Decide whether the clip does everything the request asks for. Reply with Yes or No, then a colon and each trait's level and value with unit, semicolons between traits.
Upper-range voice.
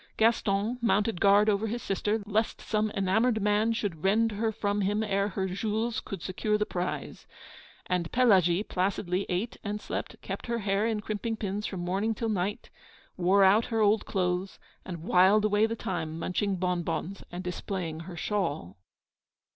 Yes: high, 200 Hz